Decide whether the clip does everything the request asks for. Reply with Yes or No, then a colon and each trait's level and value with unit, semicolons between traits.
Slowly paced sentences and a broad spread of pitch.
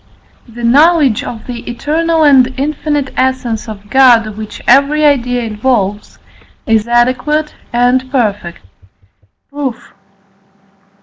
No: slow, 105 wpm; average, 3.8 semitones